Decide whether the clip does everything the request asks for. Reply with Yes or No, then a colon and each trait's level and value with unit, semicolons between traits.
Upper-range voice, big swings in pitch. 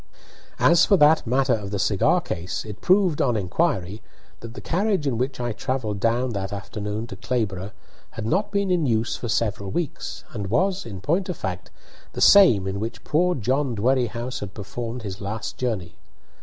No: low, 115 Hz; wide, 5.9 semitones